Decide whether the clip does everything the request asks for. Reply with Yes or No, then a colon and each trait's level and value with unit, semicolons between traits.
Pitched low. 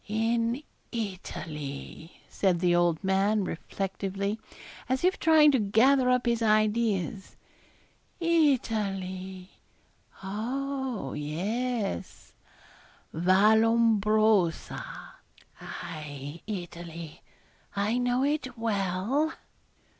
No: high, 210 Hz